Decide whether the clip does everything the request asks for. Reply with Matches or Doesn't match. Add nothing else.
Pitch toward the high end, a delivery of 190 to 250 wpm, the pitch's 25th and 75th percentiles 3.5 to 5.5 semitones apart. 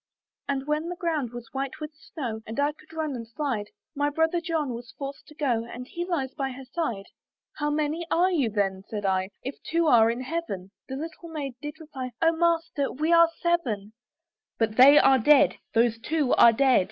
Matches